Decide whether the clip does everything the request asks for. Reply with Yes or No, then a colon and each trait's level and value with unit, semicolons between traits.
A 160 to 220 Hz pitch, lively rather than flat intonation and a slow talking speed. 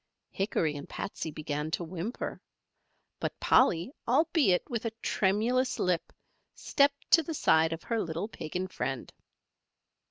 Yes: medium, 185 Hz; wide, 7.1 semitones; slow, 130 wpm